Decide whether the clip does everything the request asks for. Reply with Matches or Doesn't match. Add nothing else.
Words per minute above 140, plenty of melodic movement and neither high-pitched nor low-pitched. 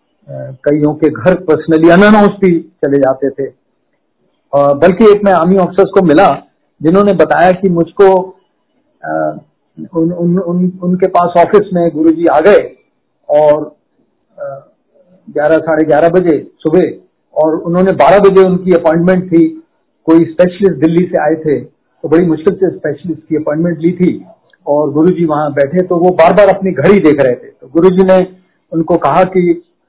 Doesn't match